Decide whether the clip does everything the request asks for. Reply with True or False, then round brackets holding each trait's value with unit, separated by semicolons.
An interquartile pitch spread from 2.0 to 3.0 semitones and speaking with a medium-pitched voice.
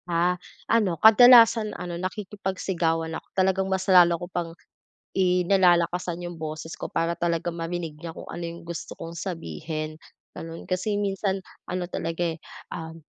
True (2.4 semitones; 175 Hz)